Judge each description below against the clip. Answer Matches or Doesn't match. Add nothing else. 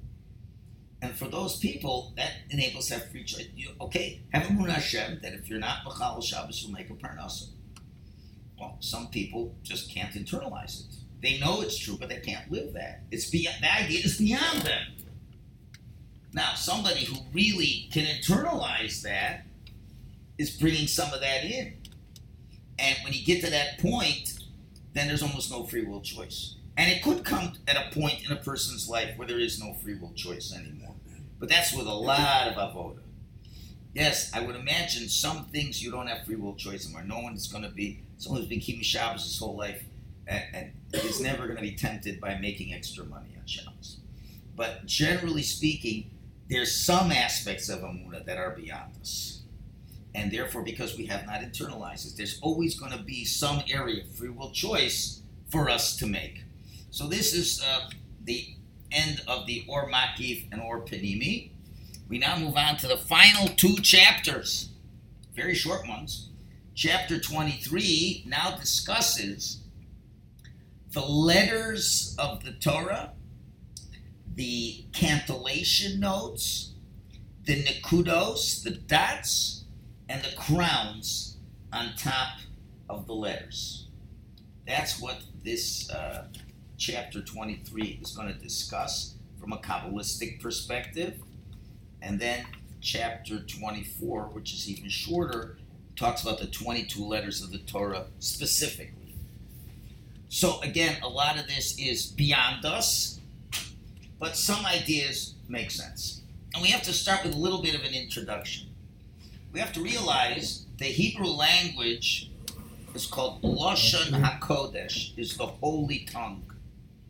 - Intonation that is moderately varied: Doesn't match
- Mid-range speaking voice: Doesn't match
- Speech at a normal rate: Matches